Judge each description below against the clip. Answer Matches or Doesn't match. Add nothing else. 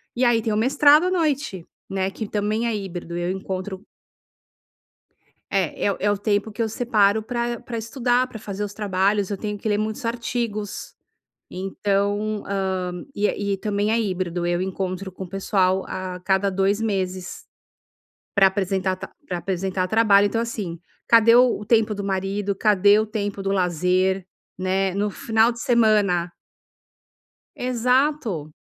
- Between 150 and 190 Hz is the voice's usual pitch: Doesn't match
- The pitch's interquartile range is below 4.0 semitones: Matches